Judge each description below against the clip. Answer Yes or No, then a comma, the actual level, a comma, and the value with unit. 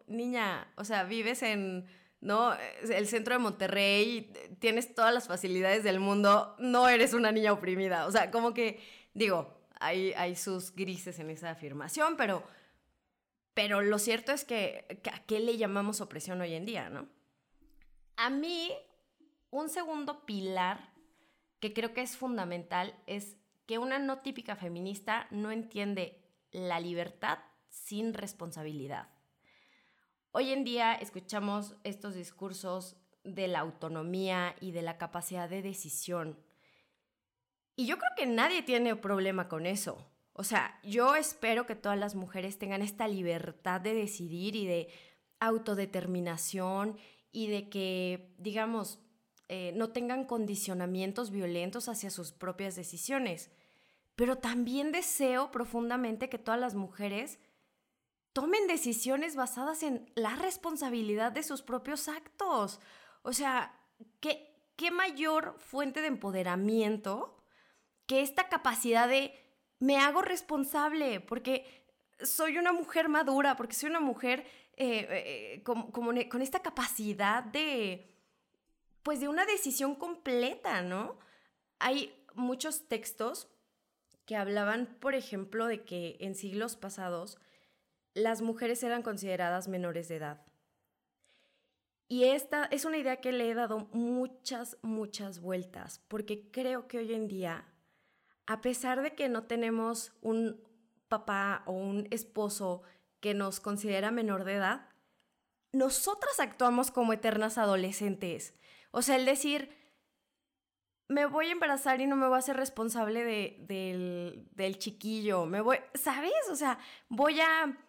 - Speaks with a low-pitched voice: No, high, 225 Hz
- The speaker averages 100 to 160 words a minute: Yes, average, 135 wpm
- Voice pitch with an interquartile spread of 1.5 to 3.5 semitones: No, average, 5.3 semitones